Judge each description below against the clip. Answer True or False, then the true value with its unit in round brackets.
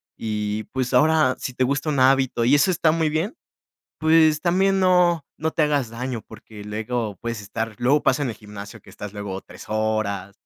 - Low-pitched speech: True (125 Hz)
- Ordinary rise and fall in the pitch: False (6.3 semitones)